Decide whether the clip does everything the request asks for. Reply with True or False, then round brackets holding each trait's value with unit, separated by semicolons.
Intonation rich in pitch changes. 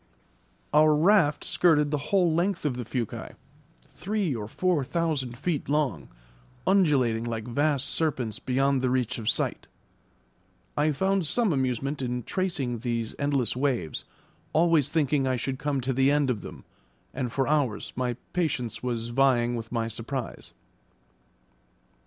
False (4.0 semitones)